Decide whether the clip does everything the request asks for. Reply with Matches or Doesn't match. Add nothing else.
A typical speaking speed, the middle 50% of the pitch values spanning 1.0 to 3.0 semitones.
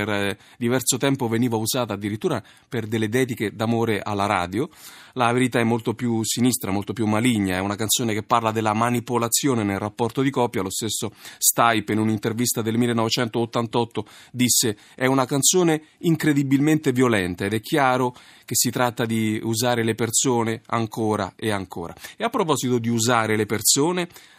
Matches